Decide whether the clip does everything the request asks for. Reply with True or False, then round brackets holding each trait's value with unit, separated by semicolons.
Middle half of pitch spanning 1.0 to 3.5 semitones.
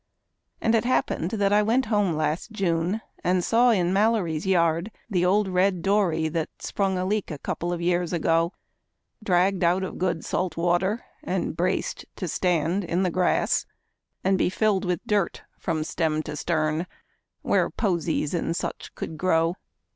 True (3.0 semitones)